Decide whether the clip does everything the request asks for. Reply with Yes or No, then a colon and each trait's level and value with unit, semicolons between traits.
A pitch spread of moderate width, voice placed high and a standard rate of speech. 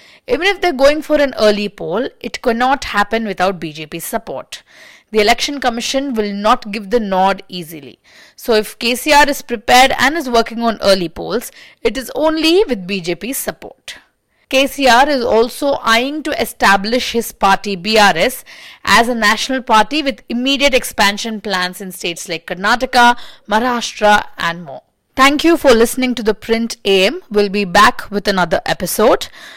Yes: average, 4.6 semitones; high, 230 Hz; average, 160 wpm